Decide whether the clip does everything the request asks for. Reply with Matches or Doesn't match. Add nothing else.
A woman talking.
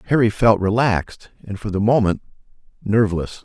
Doesn't match